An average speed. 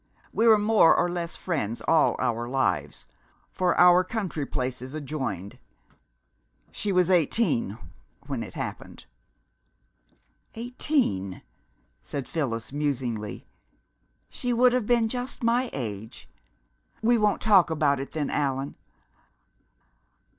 No: slow, 110 wpm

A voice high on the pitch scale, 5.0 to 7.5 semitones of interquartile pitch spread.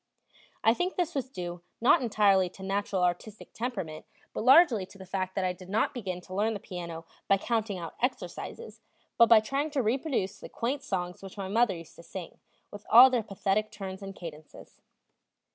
No: high, 200 Hz; average, 4.2 semitones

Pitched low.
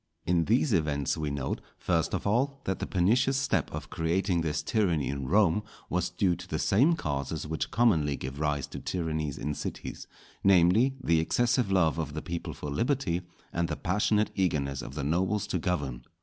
Yes: very low, 85 Hz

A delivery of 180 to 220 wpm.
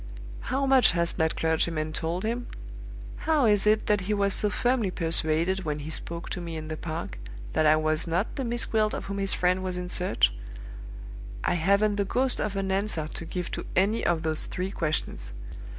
Yes: average, 200 wpm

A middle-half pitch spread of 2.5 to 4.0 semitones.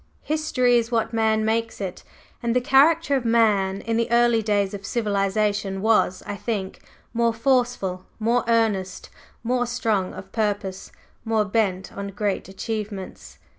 Yes: average, 3.0 semitones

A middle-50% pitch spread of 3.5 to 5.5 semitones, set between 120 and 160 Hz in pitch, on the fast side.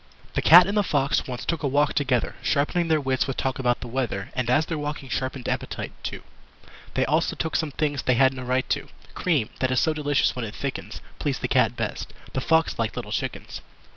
No: average, 3.1 semitones; low, 135 Hz; fast, 225 wpm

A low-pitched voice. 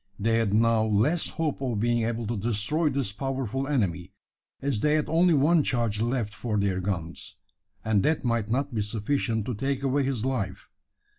Yes: low, 115 Hz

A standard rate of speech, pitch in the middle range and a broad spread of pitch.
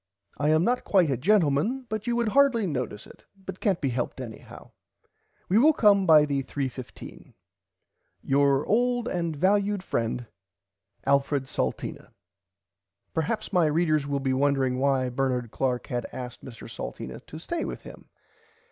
Yes: average, 155 wpm; medium, 150 Hz; wide, 7.1 semitones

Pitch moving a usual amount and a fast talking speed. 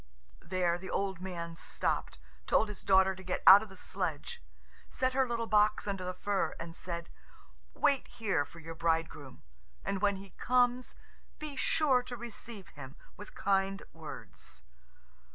No: average, 4.6 semitones; average, 155 wpm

